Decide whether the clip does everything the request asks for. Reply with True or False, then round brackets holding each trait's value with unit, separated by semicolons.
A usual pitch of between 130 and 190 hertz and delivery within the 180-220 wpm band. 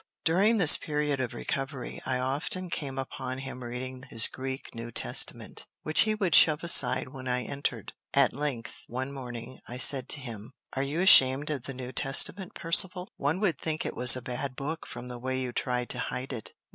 True (135 Hz; 195 wpm)